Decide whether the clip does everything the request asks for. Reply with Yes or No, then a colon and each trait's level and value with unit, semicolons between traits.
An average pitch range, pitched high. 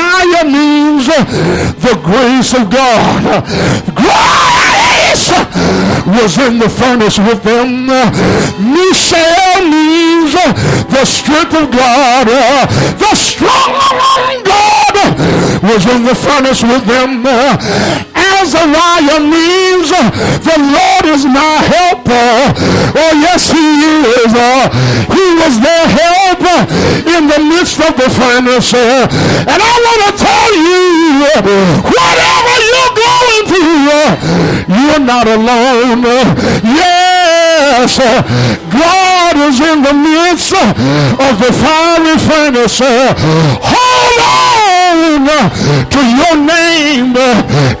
No: wide, 6.1 semitones; very high, 300 Hz